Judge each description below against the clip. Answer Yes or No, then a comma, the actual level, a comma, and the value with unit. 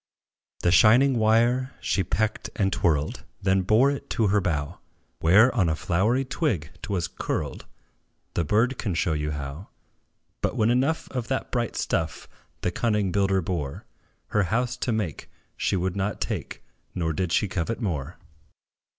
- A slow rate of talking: No, average, 160 wpm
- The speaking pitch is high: No, low, 100 Hz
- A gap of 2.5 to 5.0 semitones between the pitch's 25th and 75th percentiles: No, wide, 5.4 semitones